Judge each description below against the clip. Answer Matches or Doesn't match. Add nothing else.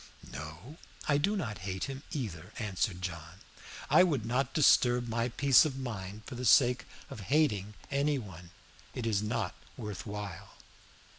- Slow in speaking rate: Doesn't match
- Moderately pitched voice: Doesn't match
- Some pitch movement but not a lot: Doesn't match